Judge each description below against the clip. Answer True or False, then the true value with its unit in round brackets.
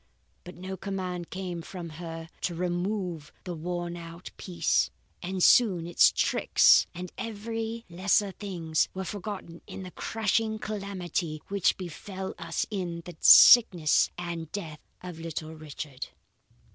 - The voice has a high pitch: False (180 Hz)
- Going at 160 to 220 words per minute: False (135 wpm)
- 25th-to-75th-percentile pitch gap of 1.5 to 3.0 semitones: True (2.7 semitones)